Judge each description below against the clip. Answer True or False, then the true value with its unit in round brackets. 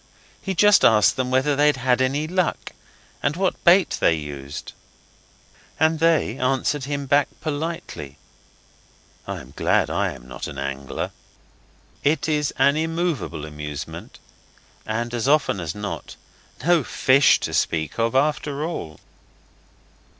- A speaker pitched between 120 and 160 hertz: True (135 Hz)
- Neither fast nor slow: False (130 wpm)